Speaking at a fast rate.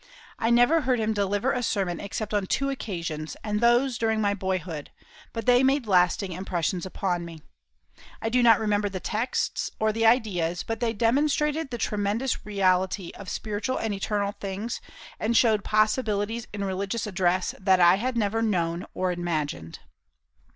No: average, 165 wpm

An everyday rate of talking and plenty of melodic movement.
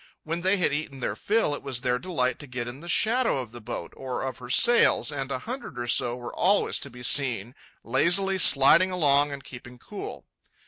No: fast, 215 wpm; wide, 6.2 semitones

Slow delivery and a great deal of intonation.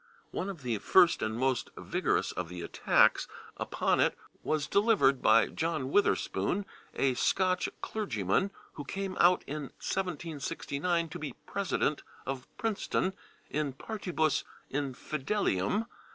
Yes: slow, 125 wpm; wide, 6.0 semitones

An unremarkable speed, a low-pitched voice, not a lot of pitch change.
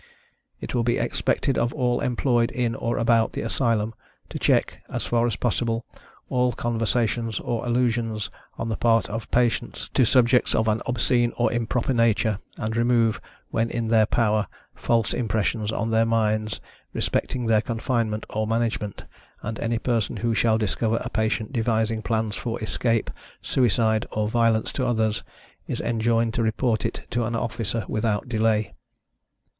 Yes: average, 160 wpm; low, 115 Hz; narrow, 1.4 semitones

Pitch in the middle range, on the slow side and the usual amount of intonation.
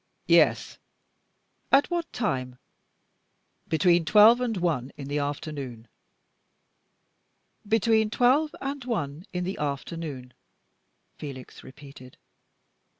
No: medium, 165 Hz; slow, 90 wpm; wide, 8.2 semitones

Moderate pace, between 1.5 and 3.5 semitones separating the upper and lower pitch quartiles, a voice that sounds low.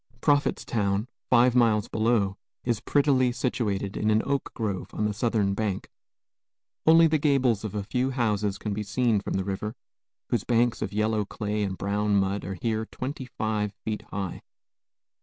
Yes: average, 165 wpm; average, 3.2 semitones; low, 110 Hz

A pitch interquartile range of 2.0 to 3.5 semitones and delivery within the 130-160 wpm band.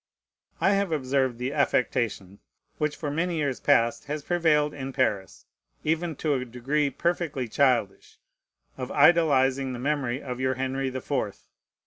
Yes: average, 3.0 semitones; average, 145 wpm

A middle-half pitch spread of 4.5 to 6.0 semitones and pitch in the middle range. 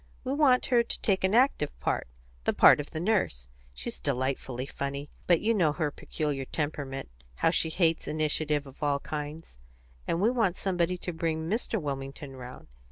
Yes: average, 5.0 semitones; medium, 155 Hz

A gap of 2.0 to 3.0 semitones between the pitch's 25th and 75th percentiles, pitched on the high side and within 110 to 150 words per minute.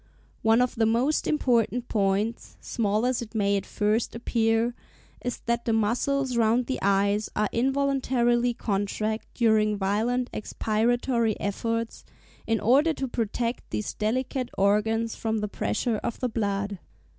Yes: narrow, 2.6 semitones; high, 225 Hz; average, 140 wpm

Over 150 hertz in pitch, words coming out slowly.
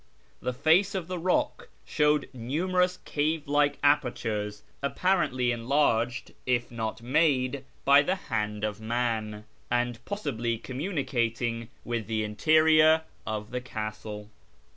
No: low, 125 Hz; slow, 120 wpm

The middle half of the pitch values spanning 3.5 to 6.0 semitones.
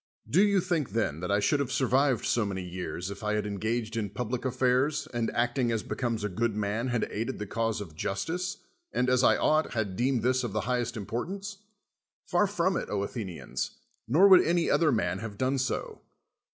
Yes: average, 4.6 semitones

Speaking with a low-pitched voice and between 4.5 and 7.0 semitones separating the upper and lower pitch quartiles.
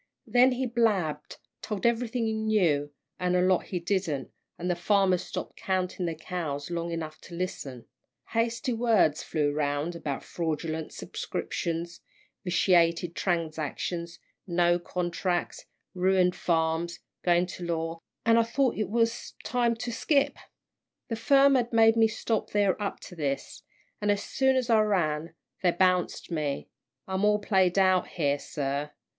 No: medium, 180 Hz; average, 4.9 semitones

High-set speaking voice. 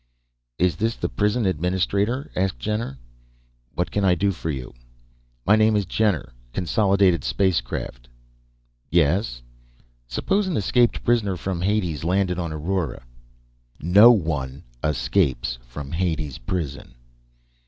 No: very low, 90 Hz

